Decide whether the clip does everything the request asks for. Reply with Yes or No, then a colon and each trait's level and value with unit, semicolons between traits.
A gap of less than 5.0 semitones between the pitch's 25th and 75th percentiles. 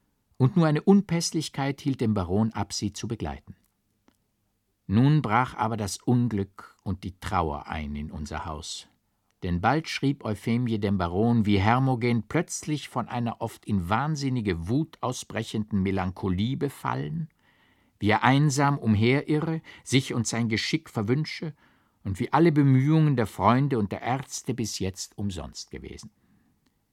No: wide, 5.4 semitones